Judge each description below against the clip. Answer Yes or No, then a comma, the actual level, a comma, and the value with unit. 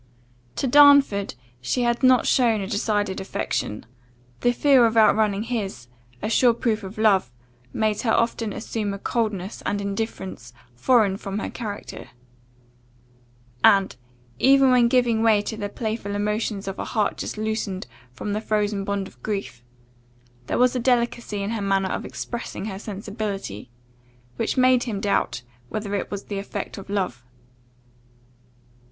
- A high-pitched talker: Yes, high, 210 Hz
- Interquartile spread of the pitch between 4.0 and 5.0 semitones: No, average, 2.8 semitones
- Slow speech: No, average, 150 wpm